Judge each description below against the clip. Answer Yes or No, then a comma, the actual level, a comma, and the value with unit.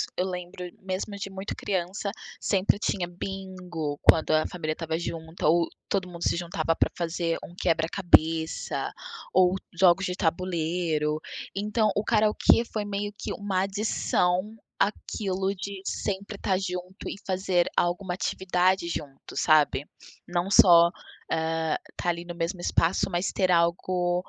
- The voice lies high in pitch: No, medium, 180 Hz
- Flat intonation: Yes, narrow, 2.3 semitones